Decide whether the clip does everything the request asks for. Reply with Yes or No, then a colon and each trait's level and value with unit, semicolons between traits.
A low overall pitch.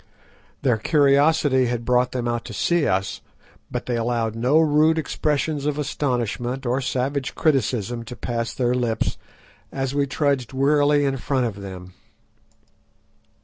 Yes: low, 130 Hz